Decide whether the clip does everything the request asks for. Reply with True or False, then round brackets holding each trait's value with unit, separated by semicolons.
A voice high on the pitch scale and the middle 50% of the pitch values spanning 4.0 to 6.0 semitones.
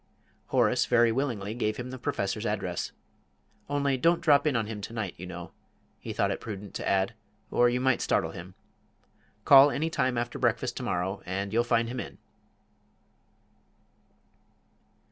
False (115 Hz; 4.6 semitones)